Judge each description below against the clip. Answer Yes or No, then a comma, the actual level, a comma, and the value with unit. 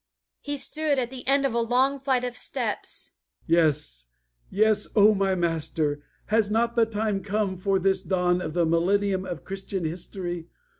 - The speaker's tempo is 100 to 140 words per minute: No, average, 165 wpm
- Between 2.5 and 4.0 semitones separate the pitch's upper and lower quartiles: No, average, 4.9 semitones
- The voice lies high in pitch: Yes, high, 195 Hz